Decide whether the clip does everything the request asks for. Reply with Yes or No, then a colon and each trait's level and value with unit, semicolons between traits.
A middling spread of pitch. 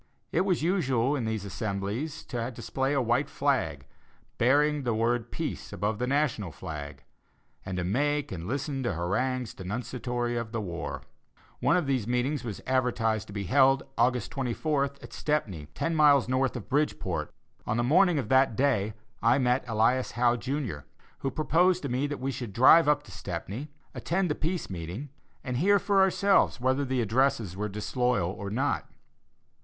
Yes: average, 4.8 semitones